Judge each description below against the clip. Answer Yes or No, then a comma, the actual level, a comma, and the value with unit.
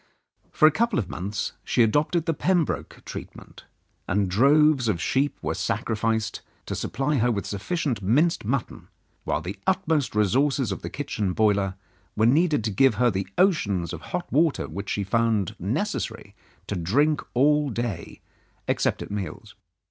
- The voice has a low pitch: Yes, low, 115 Hz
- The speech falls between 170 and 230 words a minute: No, average, 160 wpm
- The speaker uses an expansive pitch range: Yes, wide, 6.7 semitones